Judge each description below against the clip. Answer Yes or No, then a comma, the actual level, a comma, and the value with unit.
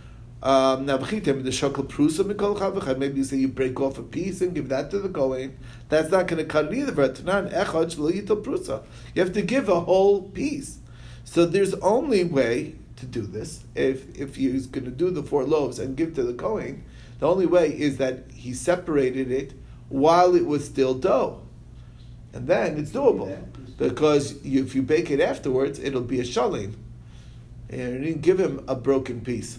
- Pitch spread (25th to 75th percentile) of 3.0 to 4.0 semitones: No, average, 5.2 semitones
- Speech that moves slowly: No, average, 175 wpm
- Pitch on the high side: No, low, 135 Hz